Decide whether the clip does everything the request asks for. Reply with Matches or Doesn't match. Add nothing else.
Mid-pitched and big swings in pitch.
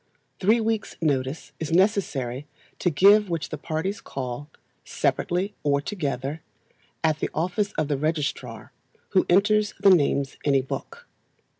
Matches